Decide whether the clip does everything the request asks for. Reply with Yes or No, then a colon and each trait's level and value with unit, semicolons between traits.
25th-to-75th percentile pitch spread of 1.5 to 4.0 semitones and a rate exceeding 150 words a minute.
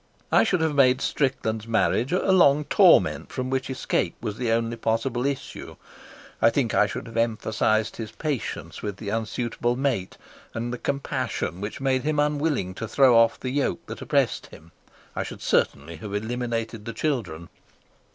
Yes: average, 3.7 semitones; average, 170 wpm